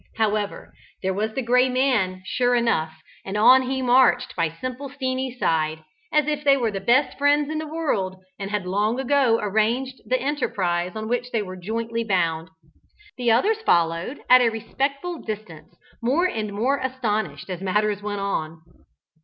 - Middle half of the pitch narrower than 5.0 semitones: No, average, 5.3 semitones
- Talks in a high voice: Yes, high, 225 Hz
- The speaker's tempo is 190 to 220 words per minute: No, average, 170 wpm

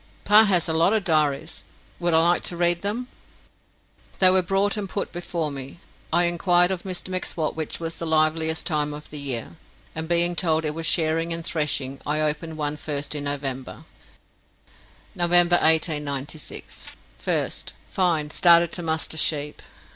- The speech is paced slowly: No, average, 160 wpm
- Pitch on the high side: No, medium, 160 Hz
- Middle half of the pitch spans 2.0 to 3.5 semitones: Yes, narrow, 2.6 semitones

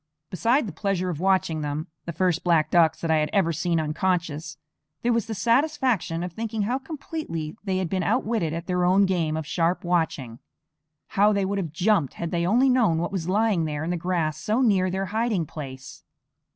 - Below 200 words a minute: No, fast, 205 wpm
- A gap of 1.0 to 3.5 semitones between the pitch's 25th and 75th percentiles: No, average, 4.2 semitones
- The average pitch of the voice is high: No, medium, 180 Hz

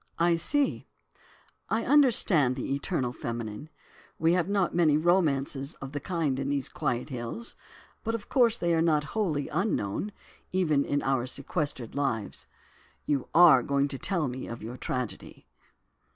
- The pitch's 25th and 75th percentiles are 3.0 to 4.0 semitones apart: No, average, 4.9 semitones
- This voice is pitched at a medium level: Yes, medium, 145 Hz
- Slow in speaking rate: No, average, 150 wpm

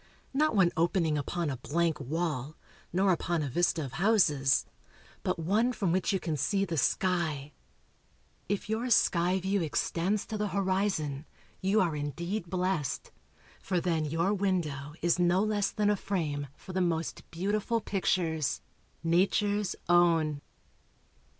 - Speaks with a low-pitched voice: No, medium, 175 Hz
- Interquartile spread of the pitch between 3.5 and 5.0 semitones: Yes, average, 3.8 semitones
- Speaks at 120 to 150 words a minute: Yes, average, 145 wpm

